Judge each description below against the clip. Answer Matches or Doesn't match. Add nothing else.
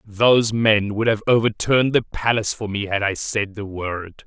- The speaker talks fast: Doesn't match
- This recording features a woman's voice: Doesn't match